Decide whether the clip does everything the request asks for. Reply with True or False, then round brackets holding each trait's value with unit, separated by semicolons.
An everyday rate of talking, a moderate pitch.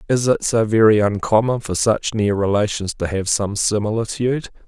False (165 wpm; 110 Hz)